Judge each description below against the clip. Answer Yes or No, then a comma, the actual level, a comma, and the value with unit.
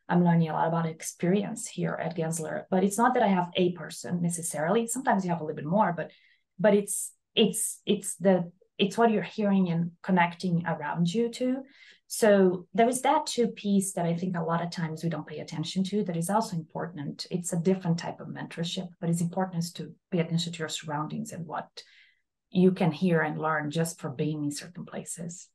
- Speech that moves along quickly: Yes, fast, 210 wpm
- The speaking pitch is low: No, medium, 180 Hz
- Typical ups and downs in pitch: Yes, average, 3.8 semitones